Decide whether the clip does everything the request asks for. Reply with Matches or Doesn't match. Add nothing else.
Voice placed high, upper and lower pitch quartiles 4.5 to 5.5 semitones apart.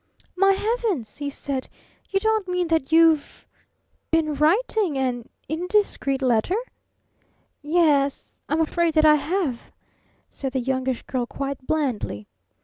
Matches